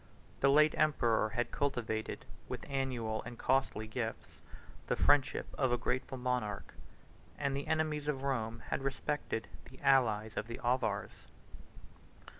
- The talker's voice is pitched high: No, low, 125 Hz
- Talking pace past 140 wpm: No, slow, 135 wpm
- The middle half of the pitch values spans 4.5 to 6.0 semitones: No, average, 3.6 semitones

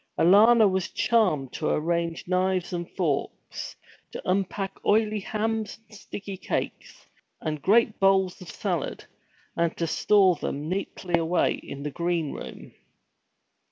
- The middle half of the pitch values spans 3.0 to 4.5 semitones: Yes, average, 3.5 semitones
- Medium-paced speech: No, slow, 130 wpm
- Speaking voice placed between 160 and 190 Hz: Yes, medium, 185 Hz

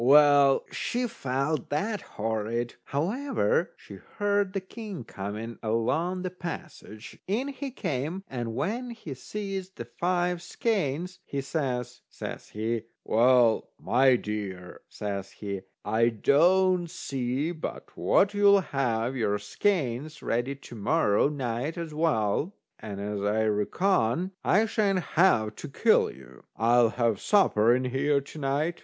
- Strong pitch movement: Yes, wide, 8.2 semitones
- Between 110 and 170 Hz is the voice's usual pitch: Yes, medium, 140 Hz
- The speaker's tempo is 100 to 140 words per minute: Yes, slow, 135 wpm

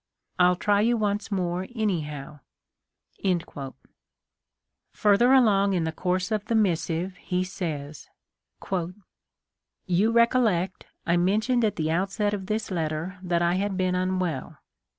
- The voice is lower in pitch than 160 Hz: No, medium, 185 Hz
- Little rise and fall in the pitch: No, average, 3.3 semitones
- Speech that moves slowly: Yes, slow, 130 wpm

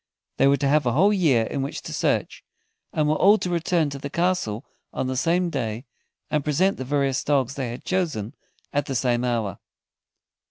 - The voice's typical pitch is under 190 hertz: Yes, medium, 140 Hz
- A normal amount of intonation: Yes, average, 4.8 semitones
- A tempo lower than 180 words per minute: No, average, 200 wpm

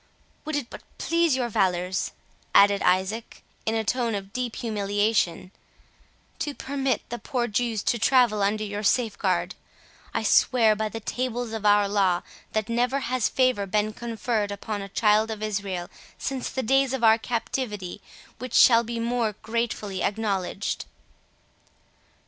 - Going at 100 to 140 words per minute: No, average, 150 wpm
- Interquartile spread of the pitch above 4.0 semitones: No, average, 3.1 semitones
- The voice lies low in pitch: No, high, 220 Hz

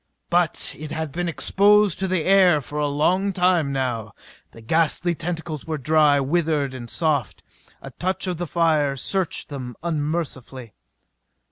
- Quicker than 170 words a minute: No, average, 150 wpm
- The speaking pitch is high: No, medium, 155 Hz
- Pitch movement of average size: Yes, average, 3.8 semitones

